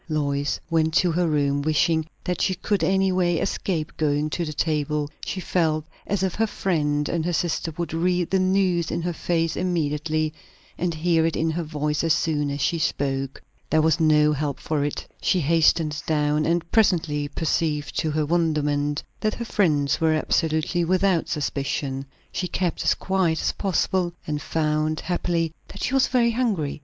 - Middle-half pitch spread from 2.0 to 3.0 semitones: Yes, average, 2.7 semitones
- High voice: No, medium, 160 Hz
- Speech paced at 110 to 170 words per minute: No, average, 180 wpm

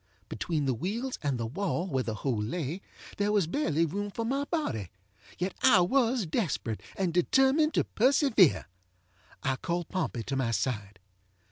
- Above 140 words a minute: Yes, average, 155 wpm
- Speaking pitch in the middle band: Yes, medium, 175 Hz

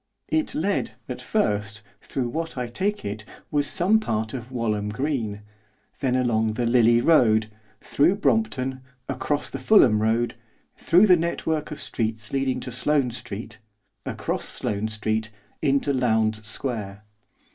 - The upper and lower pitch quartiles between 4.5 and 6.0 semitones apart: Yes, average, 5.1 semitones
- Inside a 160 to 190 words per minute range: No, average, 140 wpm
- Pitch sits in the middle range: No, low, 120 Hz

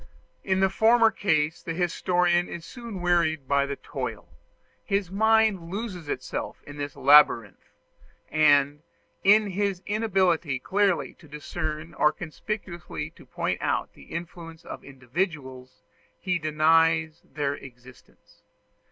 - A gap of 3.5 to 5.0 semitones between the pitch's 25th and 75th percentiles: Yes, average, 4.5 semitones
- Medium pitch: Yes, medium, 165 Hz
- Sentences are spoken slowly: Yes, slow, 125 wpm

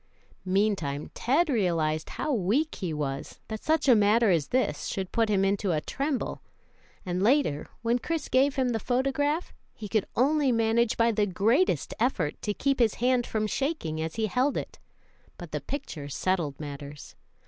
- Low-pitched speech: No, high, 220 Hz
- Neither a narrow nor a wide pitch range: No, wide, 6.8 semitones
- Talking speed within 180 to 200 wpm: No, average, 170 wpm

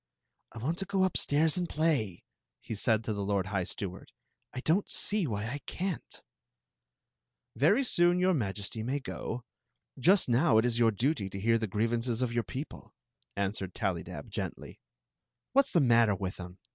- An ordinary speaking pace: Yes, average, 185 wpm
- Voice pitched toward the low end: Yes, low, 120 Hz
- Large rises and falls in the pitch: Yes, wide, 7.4 semitones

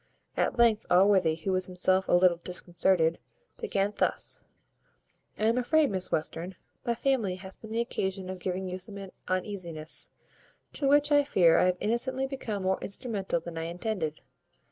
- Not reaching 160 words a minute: No, average, 165 wpm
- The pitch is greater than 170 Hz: Yes, high, 190 Hz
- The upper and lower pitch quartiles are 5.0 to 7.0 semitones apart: No, average, 4.0 semitones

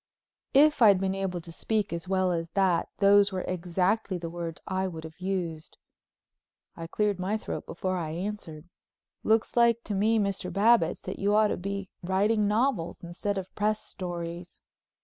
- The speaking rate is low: No, average, 170 wpm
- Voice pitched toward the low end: No, high, 190 Hz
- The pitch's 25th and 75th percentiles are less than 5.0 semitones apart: Yes, average, 3.3 semitones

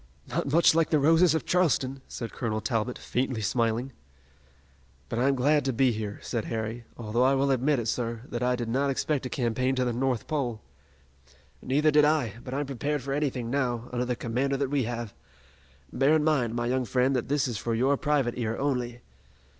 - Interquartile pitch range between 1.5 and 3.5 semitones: Yes, average, 3.0 semitones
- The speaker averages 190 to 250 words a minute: Yes, average, 200 wpm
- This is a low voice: Yes, low, 130 Hz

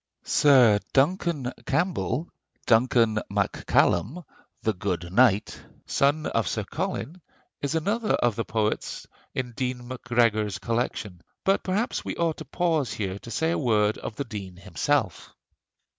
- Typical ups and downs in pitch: No, wide, 6.4 semitones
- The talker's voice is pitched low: Yes, low, 120 Hz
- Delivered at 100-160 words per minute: Yes, average, 140 wpm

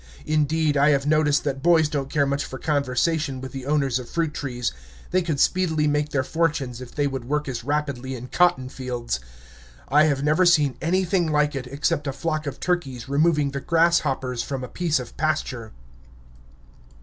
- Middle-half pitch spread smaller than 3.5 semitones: Yes, average, 2.8 semitones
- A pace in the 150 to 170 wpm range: No, average, 185 wpm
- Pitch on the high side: No, medium, 145 Hz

